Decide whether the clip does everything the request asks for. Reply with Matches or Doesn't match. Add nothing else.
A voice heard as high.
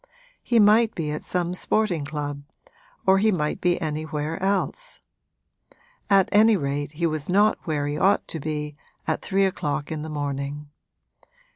Doesn't match